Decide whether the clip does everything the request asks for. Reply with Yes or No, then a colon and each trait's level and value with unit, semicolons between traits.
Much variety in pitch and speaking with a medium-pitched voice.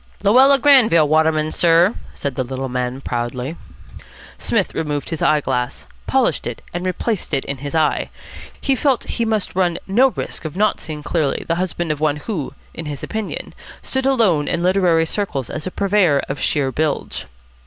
Yes: wide, 5.7 semitones; medium, 165 Hz